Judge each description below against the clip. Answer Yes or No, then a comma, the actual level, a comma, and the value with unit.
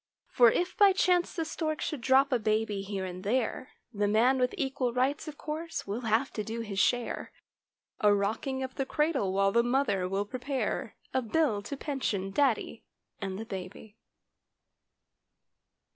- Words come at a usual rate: Yes, average, 170 wpm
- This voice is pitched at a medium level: No, high, 240 Hz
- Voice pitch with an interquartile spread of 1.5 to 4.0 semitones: No, average, 5.1 semitones